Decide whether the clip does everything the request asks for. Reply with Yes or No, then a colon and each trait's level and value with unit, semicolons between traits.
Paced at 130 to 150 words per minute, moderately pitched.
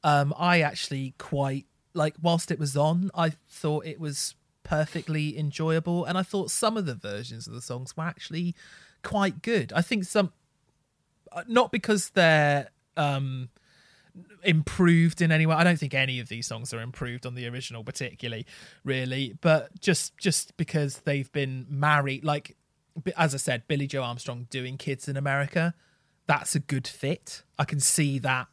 No: average, 170 wpm; medium, 150 Hz